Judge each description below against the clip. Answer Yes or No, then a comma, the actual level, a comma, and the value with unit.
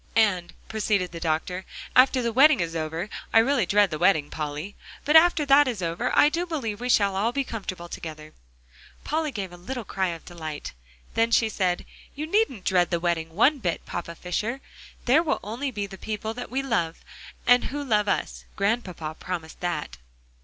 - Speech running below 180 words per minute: No, average, 190 wpm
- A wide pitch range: Yes, wide, 6.4 semitones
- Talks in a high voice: Yes, high, 205 Hz